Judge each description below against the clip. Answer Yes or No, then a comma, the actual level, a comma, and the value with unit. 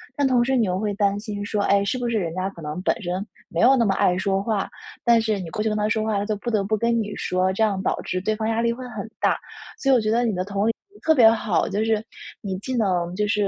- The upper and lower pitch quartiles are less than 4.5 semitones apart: Yes, average, 2.7 semitones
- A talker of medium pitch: No, high, 210 Hz